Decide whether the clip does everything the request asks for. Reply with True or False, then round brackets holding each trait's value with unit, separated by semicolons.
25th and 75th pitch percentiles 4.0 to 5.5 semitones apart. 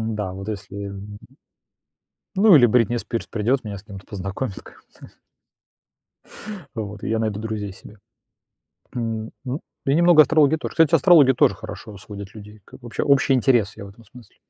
True (4.5 semitones)